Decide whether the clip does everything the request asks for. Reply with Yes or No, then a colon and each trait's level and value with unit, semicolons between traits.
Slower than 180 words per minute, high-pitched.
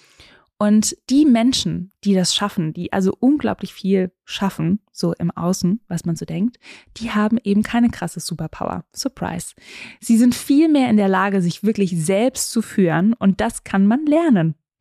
Yes: average, 165 wpm; high, 200 Hz